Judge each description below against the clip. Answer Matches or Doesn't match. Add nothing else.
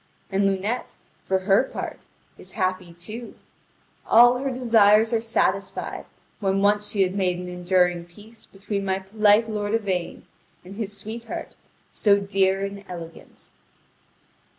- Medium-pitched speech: Doesn't match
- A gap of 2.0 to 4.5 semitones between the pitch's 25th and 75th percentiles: Matches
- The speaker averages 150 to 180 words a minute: Doesn't match